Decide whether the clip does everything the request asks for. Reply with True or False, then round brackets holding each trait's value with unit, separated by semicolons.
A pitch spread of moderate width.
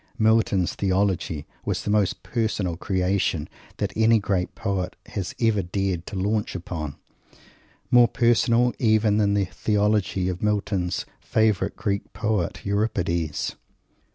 True (3.0 semitones)